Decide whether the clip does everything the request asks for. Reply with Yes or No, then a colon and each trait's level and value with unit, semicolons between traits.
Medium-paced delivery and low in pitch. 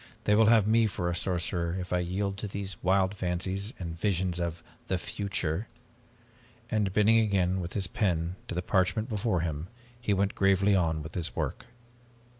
Yes: average, 180 wpm; very low, 95 Hz